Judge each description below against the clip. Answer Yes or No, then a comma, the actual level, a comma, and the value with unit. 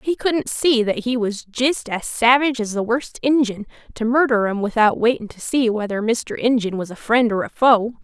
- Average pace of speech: No, fast, 215 wpm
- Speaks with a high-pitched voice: Yes, high, 235 Hz